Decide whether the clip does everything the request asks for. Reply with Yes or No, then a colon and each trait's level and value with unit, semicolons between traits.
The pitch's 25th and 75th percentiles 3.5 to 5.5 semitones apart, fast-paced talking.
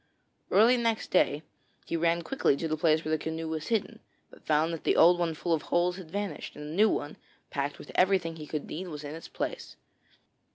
No: average, 3.0 semitones; fast, 220 wpm